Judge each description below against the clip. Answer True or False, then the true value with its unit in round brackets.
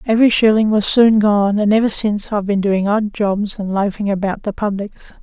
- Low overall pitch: False (205 Hz)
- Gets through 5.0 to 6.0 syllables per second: True (5.4 syllables/s)